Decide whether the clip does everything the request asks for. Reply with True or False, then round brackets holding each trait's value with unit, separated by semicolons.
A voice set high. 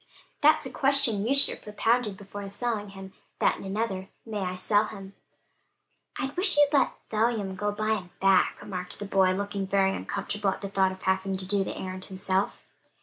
True (200 Hz)